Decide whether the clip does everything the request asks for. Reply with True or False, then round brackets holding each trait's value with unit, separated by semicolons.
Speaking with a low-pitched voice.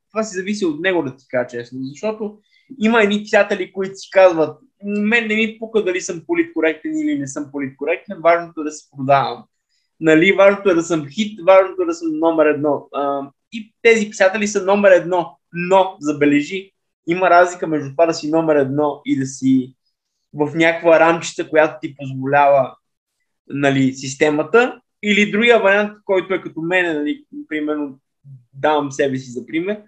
False (170 Hz)